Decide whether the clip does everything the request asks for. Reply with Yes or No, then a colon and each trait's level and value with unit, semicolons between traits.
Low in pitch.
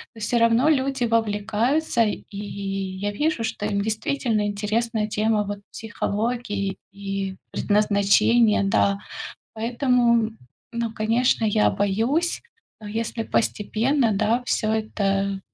No: high, 220 Hz